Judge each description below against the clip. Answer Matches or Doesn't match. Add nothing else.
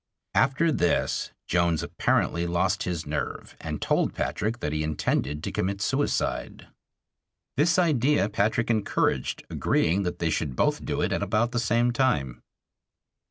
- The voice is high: Doesn't match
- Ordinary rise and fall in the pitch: Doesn't match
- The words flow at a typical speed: Matches